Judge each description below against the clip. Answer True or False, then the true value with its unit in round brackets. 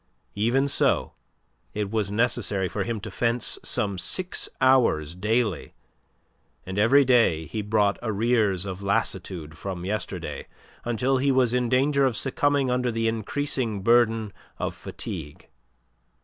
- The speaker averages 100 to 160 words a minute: True (135 wpm)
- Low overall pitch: True (115 Hz)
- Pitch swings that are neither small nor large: True (4.0 semitones)